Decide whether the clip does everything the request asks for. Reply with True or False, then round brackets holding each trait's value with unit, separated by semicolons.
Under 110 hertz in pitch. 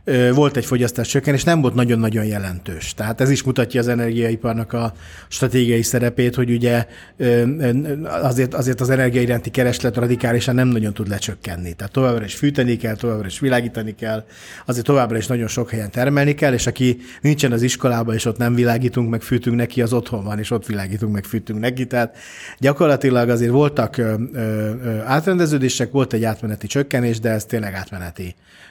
False (120 Hz)